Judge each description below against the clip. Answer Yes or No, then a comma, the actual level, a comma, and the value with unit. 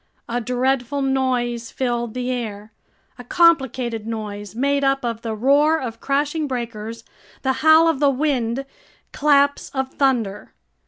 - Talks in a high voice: Yes, very high, 255 Hz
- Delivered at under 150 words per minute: Yes, average, 140 wpm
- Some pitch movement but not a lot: Yes, average, 3.4 semitones